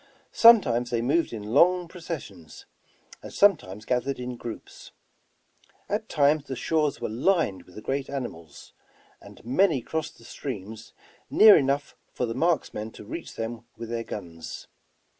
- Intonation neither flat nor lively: No, wide, 5.9 semitones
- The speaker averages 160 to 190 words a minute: No, average, 150 wpm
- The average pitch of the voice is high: No, low, 125 Hz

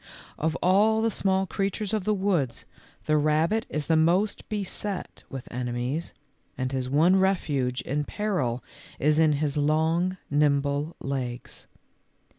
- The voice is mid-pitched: Yes, medium, 155 Hz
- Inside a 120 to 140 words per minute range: Yes, slow, 135 wpm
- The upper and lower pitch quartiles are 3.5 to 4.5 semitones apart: No, average, 5.2 semitones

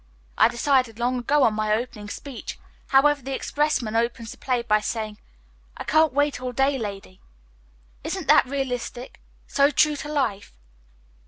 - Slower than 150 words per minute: No, average, 155 wpm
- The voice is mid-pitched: No, very high, 250 Hz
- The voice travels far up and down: No, average, 4.0 semitones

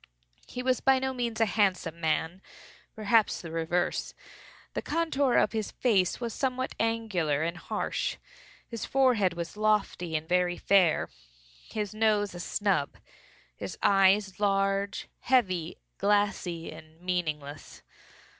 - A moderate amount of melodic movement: Yes, average, 4.4 semitones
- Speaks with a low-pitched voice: No, high, 195 Hz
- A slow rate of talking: Yes, slow, 125 wpm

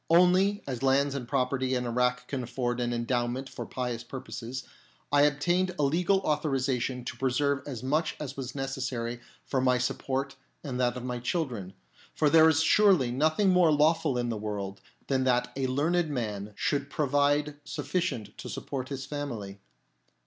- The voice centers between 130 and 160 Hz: Yes, low, 135 Hz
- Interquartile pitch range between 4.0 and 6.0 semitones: No, average, 3.1 semitones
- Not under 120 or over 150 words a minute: No, average, 165 wpm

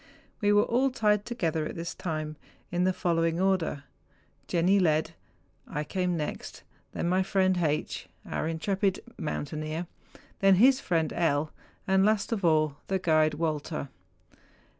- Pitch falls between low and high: Yes, medium, 175 Hz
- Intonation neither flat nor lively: Yes, average, 3.8 semitones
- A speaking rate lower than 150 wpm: Yes, average, 140 wpm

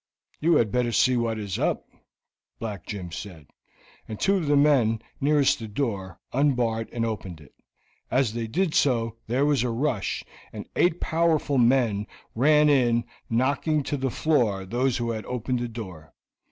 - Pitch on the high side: No, low, 120 Hz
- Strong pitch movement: No, average, 4.4 semitones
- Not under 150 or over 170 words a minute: Yes, average, 165 wpm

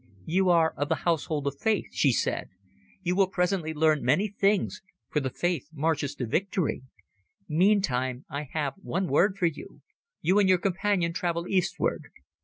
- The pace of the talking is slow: No, average, 165 wpm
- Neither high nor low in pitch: Yes, medium, 170 Hz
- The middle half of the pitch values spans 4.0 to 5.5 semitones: Yes, average, 4.3 semitones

